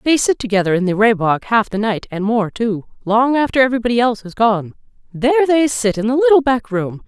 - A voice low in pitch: No, high, 230 Hz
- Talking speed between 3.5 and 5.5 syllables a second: No, 5.8 syllables/s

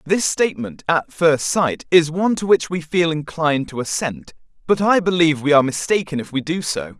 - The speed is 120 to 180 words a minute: No, fast, 205 wpm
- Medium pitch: Yes, medium, 160 Hz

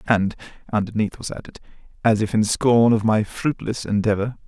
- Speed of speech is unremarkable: Yes, average, 160 wpm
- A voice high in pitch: No, low, 110 Hz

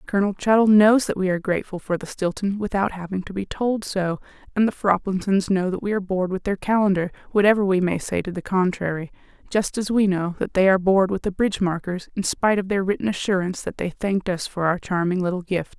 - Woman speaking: Yes, female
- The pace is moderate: No, fast, 230 wpm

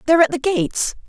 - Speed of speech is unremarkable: No, fast, 220 wpm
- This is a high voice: Yes, very high, 300 Hz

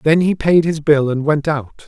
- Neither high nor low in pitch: Yes, medium, 150 Hz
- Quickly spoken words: Yes, fast, 255 wpm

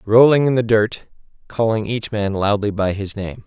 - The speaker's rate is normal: Yes, average, 190 wpm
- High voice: No, low, 110 Hz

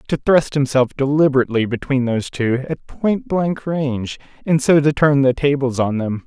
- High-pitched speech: No, medium, 140 Hz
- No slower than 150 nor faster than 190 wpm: Yes, average, 170 wpm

